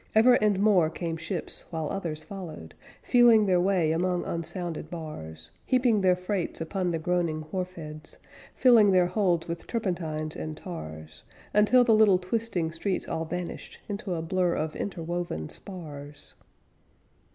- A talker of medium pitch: Yes, medium, 175 Hz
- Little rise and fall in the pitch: No, average, 3.6 semitones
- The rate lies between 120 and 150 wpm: Yes, average, 145 wpm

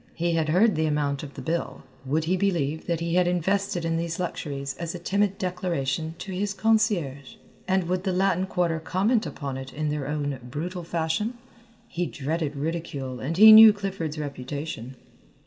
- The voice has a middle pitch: Yes, medium, 165 Hz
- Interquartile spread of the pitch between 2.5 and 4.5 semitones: Yes, average, 4.0 semitones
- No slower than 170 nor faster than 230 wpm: Yes, average, 180 wpm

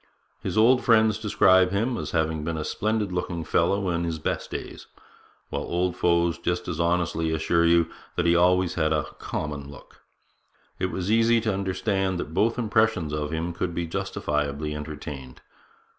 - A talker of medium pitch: No, very low, 85 Hz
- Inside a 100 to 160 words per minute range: No, average, 170 wpm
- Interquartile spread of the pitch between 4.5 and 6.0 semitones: No, average, 3.5 semitones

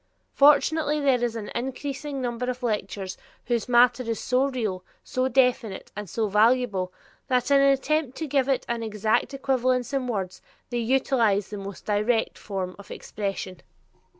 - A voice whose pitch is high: Yes, high, 245 Hz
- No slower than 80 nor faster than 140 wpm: No, average, 160 wpm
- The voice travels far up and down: No, average, 4.2 semitones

